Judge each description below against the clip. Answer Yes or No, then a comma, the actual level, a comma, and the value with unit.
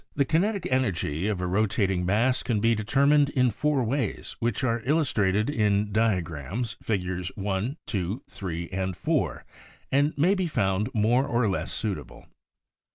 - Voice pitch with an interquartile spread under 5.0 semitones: No, wide, 5.5 semitones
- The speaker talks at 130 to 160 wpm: Yes, average, 150 wpm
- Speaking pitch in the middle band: No, low, 110 Hz